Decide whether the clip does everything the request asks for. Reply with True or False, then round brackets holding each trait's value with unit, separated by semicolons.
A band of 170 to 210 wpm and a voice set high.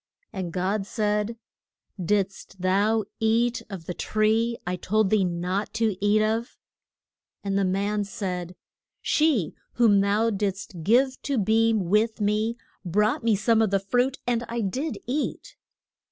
False (150 wpm; 210 Hz)